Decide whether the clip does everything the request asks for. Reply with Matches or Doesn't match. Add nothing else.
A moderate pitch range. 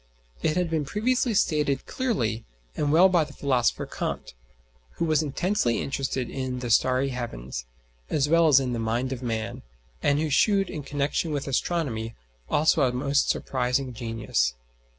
Matches